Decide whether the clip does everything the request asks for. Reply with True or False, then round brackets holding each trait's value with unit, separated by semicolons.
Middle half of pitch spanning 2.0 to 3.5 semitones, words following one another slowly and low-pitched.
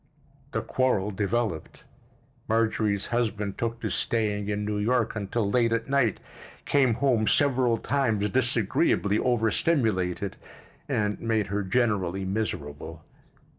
True (3.0 semitones; 115 wpm; 110 Hz)